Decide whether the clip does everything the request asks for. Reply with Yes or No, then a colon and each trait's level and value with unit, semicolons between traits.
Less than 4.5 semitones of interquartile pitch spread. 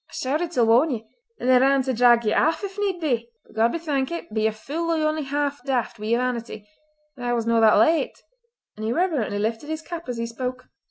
No: average, 5.1 semitones